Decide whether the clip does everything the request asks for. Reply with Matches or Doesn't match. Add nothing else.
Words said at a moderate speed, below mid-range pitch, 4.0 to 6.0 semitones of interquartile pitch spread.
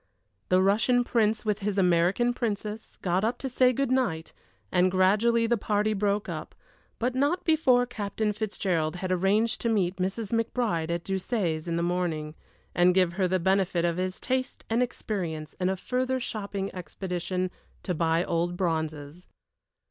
Doesn't match